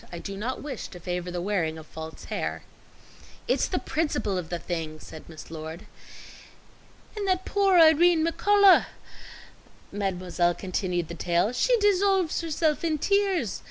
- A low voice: No, high, 205 Hz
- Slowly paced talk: No, average, 150 wpm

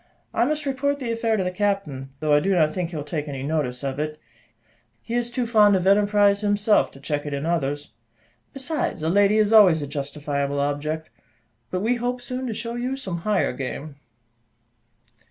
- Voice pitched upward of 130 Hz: Yes, medium, 185 Hz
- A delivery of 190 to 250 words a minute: Yes, average, 195 wpm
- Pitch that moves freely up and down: Yes, wide, 7.5 semitones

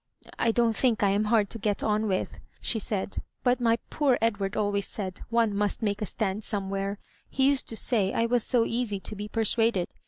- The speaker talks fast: Yes, fast, 220 wpm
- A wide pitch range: No, narrow, 2.4 semitones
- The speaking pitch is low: No, high, 215 Hz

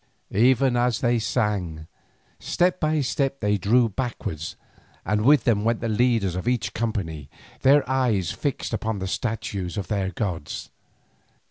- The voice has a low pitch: Yes, low, 110 Hz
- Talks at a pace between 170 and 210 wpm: No, average, 145 wpm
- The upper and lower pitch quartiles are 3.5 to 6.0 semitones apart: Yes, average, 4.4 semitones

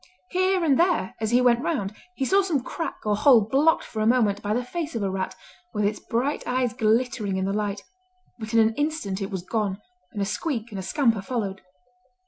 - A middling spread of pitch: Yes, average, 5.0 semitones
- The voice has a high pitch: Yes, high, 225 Hz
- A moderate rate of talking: No, fast, 220 wpm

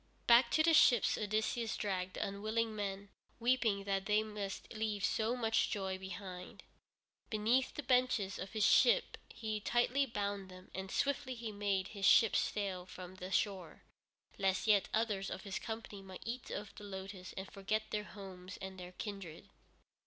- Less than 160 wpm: No, average, 165 wpm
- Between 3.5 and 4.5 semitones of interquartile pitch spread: No, average, 2.7 semitones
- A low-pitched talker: No, high, 205 Hz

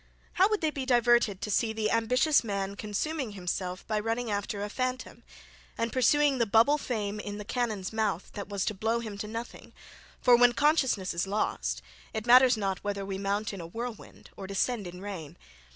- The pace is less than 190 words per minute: No, average, 195 wpm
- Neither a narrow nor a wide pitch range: Yes, average, 3.4 semitones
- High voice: Yes, high, 220 Hz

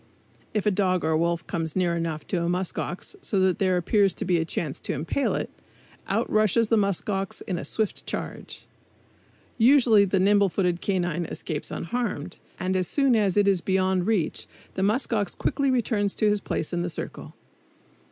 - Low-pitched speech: No, high, 190 Hz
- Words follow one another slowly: No, average, 190 wpm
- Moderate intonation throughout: Yes, average, 3.2 semitones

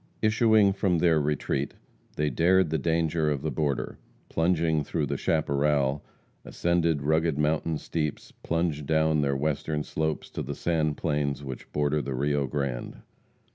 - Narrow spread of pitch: Yes, narrow, 2.3 semitones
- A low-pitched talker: Yes, very low, 75 Hz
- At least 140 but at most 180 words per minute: Yes, average, 145 wpm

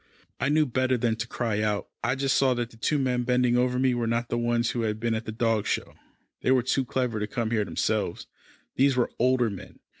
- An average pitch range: No, narrow, 2.2 semitones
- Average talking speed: No, fast, 240 wpm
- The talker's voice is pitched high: No, low, 120 Hz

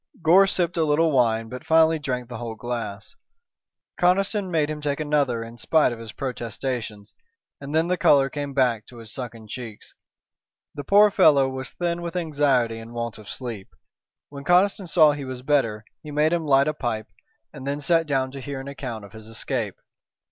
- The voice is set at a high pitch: No, low, 135 Hz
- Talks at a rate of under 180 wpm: No, average, 190 wpm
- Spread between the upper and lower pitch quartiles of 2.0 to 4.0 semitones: No, average, 5.1 semitones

